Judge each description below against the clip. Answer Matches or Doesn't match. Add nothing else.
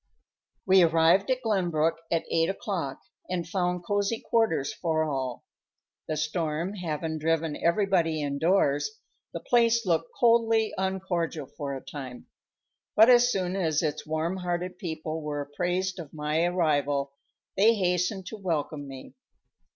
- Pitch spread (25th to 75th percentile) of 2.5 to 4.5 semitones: Matches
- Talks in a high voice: Doesn't match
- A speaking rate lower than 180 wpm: Matches